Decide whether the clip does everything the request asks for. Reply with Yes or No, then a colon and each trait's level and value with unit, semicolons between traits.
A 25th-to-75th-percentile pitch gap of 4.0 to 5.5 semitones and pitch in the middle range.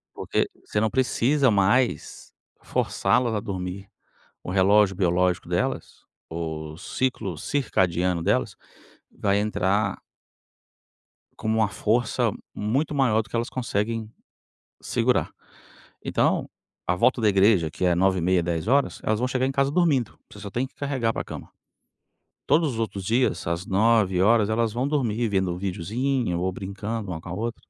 No: average, 4.4 semitones; low, 105 Hz